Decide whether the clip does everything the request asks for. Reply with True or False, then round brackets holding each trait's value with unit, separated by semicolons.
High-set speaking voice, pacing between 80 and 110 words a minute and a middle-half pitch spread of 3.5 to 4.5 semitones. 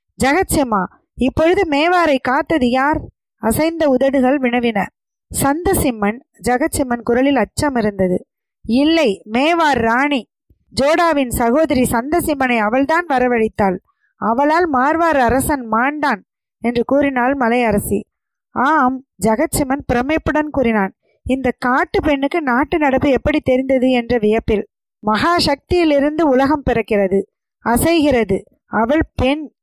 True (265 Hz; 95 wpm; 4.2 semitones)